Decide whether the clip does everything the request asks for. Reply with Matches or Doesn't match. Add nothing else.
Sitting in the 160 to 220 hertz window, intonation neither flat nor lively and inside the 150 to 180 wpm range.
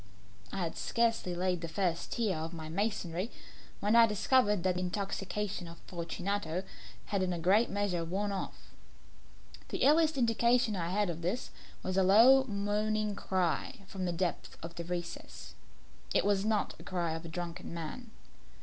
Matches